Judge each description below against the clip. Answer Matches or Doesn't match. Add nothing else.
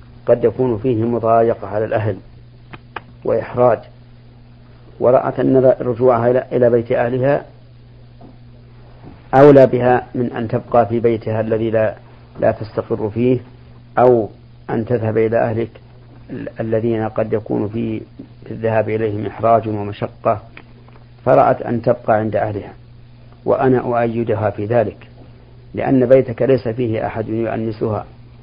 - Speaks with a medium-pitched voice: Doesn't match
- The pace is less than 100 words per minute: Doesn't match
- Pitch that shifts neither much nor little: Doesn't match